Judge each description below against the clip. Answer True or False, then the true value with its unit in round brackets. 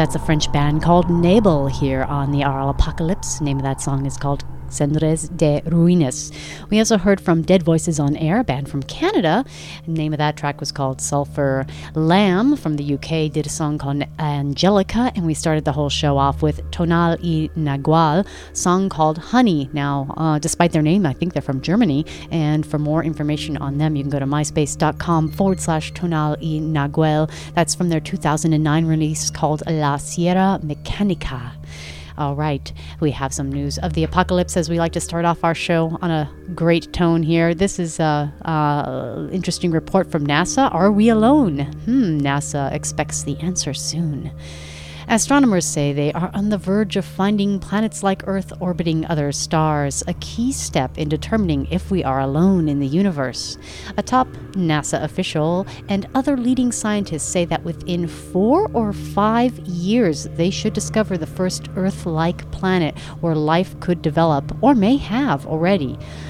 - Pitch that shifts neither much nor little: True (3.7 semitones)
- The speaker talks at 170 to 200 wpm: True (175 wpm)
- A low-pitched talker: False (160 Hz)